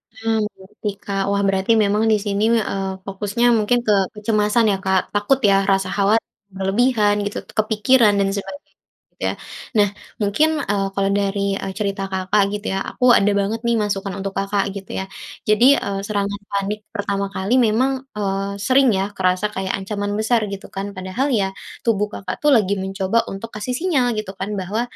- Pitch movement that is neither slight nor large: No, narrow, 1.8 semitones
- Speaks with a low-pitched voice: No, high, 205 Hz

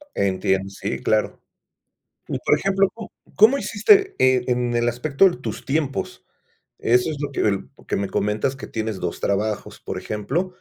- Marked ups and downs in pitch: Yes, wide, 8.3 semitones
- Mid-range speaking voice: No, low, 125 Hz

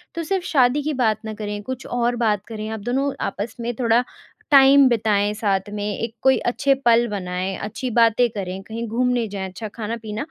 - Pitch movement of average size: Yes, average, 3.0 semitones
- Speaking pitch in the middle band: No, high, 230 Hz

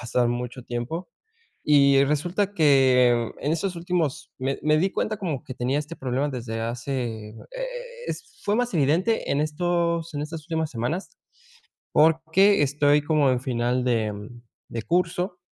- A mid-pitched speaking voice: Yes, medium, 145 Hz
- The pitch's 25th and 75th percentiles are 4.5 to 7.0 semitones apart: Yes, average, 5.1 semitones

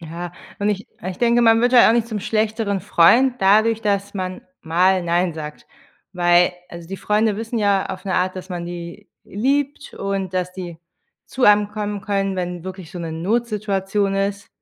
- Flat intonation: No, average, 3.1 semitones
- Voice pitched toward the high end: Yes, high, 195 Hz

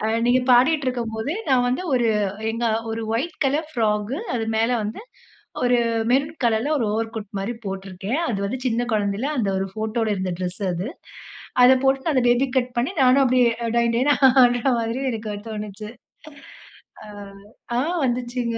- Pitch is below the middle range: No, high, 235 Hz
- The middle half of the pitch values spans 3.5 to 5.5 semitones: No, average, 2.8 semitones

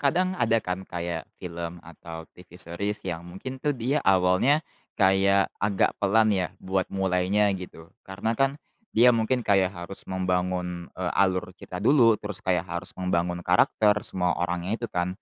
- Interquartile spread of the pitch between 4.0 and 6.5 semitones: No, average, 3.3 semitones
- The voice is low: Yes, very low, 95 Hz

